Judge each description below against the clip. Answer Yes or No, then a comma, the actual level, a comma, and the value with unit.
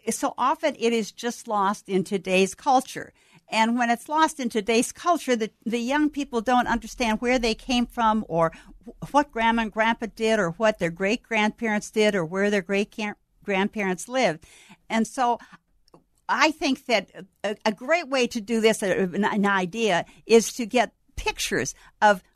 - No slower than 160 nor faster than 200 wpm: Yes, average, 170 wpm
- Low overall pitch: No, high, 225 Hz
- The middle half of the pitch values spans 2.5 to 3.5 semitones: Yes, average, 3.0 semitones